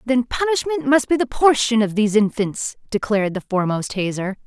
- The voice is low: No, high, 230 Hz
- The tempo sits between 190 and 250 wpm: No, average, 175 wpm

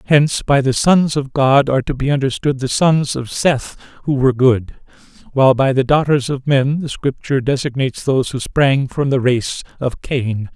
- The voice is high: No, low, 135 Hz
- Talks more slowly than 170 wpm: No, average, 195 wpm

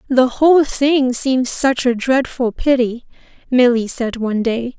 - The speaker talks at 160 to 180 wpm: No, average, 150 wpm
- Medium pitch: No, very high, 250 Hz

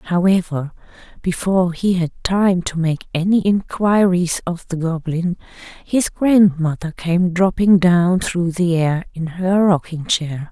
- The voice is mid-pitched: Yes, medium, 175 Hz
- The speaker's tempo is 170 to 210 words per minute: No, slow, 135 wpm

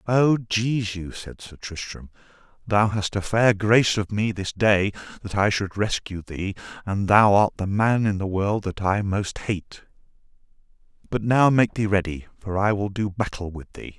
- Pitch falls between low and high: No, low, 100 Hz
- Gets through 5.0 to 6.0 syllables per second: No, 4.5 syllables/s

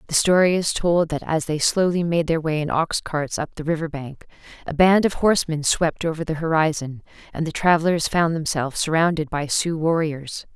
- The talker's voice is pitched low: No, medium, 160 Hz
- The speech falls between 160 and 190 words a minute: No, average, 200 wpm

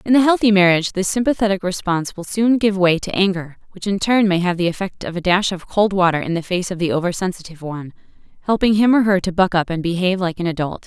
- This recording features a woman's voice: Yes, female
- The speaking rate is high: Yes, fast, 250 wpm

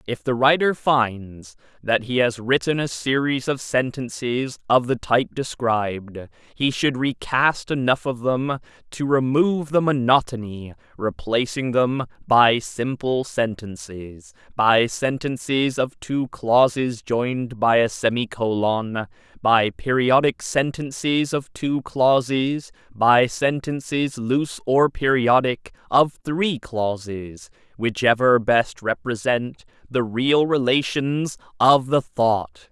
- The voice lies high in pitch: No, low, 125 Hz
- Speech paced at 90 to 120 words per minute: Yes, slow, 115 wpm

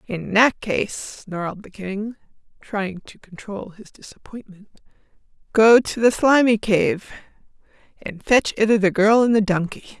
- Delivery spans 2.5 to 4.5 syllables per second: Yes, 4.2 syllables/s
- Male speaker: No, female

